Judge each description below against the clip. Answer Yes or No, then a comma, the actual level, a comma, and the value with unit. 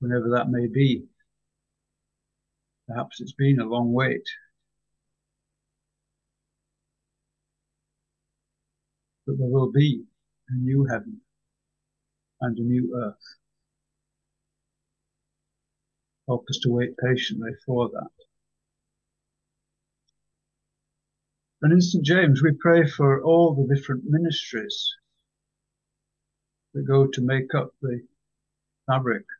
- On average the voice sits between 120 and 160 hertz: Yes, low, 135 Hz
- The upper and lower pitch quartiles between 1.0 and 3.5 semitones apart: No, average, 4.5 semitones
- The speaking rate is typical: No, slow, 95 wpm